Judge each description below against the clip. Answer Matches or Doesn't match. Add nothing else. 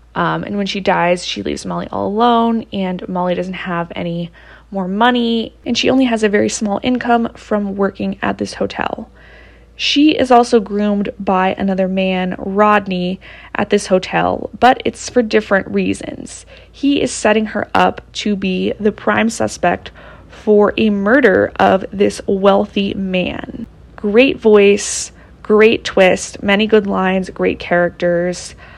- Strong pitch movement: Doesn't match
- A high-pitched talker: Matches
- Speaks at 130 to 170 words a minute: Matches